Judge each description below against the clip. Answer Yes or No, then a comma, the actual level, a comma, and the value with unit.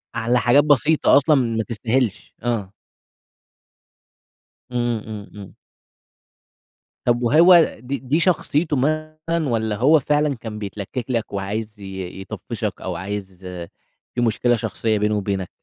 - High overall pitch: No, low, 120 Hz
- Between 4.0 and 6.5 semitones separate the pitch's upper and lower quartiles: Yes, wide, 5.4 semitones